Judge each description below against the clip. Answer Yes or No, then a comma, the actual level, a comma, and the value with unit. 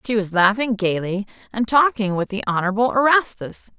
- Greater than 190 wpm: No, average, 160 wpm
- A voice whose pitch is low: No, high, 215 Hz